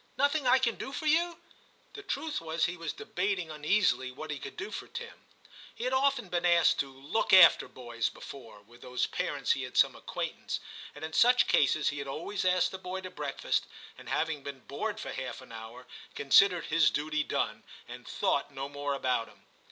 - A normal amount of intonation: No, wide, 7.4 semitones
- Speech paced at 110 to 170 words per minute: No, average, 200 wpm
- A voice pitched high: No, medium, 160 Hz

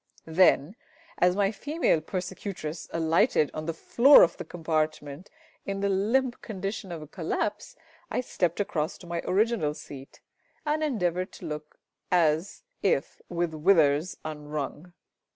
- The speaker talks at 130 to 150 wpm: Yes, slow, 135 wpm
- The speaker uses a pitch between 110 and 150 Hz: No, medium, 175 Hz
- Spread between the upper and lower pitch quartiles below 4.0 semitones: No, average, 4.3 semitones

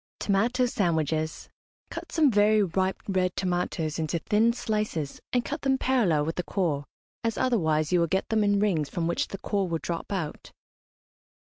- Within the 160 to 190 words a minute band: Yes, average, 175 wpm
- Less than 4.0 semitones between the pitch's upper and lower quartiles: No, average, 4.7 semitones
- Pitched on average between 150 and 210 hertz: Yes, high, 190 Hz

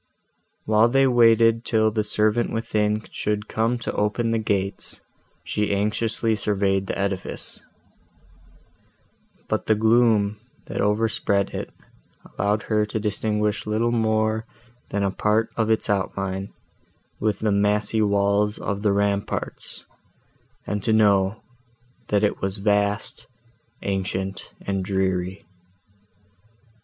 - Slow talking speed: Yes, slow, 120 wpm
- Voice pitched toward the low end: Yes, low, 105 Hz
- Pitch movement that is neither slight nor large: No, narrow, 1.7 semitones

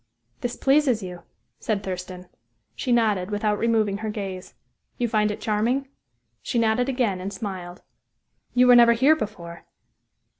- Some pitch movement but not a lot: Yes, average, 3.9 semitones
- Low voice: No, high, 215 Hz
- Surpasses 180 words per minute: No, average, 145 wpm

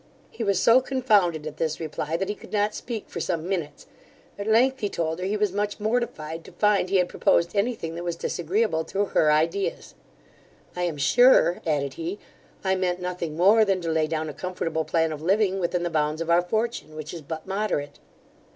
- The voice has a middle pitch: Yes, medium, 180 Hz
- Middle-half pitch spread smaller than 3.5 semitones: No, average, 4.3 semitones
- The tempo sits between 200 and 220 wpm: Yes, fast, 205 wpm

